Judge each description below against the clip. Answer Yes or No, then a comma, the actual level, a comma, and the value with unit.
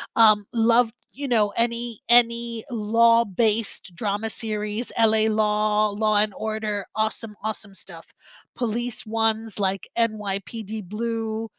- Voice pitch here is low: No, high, 220 Hz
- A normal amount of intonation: No, narrow, 1.6 semitones